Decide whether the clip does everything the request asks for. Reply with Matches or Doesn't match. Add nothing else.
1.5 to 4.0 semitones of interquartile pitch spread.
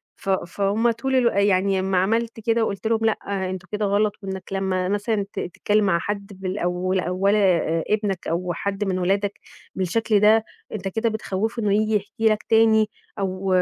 Matches